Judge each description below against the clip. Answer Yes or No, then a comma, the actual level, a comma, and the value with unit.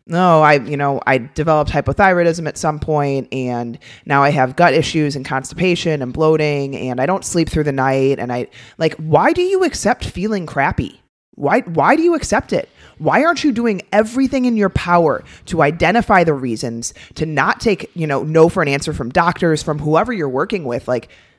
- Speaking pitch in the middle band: Yes, medium, 155 Hz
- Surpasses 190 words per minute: Yes, average, 200 wpm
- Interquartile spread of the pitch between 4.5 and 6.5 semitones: Yes, average, 5.0 semitones